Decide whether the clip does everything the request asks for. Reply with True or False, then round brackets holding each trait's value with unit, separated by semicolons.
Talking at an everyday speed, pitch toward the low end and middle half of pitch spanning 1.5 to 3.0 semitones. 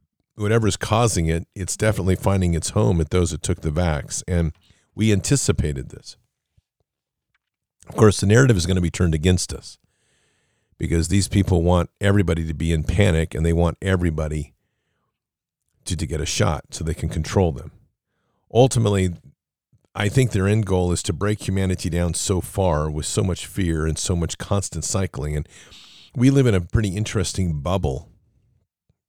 False (170 wpm; 90 Hz; 3.8 semitones)